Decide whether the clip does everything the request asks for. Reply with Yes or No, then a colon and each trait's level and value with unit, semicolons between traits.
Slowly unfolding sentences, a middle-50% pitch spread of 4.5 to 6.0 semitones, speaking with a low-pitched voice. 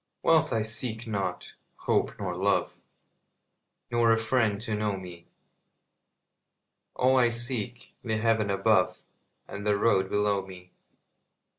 No: slow, 125 wpm; average, 2.8 semitones; low, 110 Hz